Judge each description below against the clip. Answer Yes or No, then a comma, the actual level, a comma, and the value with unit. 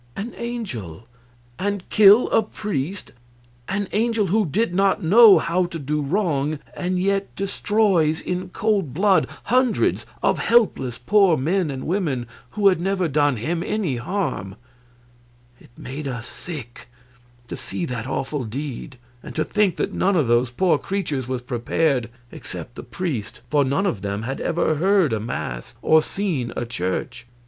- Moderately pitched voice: Yes, medium, 160 Hz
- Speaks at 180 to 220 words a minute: No, average, 155 wpm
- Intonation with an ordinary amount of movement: No, wide, 7.4 semitones